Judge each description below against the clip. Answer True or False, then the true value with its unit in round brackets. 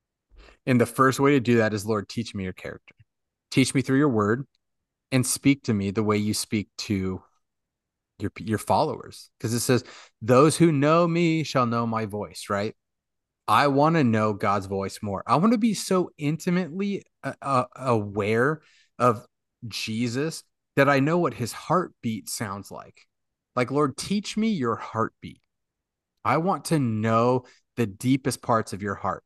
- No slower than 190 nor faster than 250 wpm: False (170 wpm)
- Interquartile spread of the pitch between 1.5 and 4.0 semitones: False (5.2 semitones)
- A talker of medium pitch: False (120 Hz)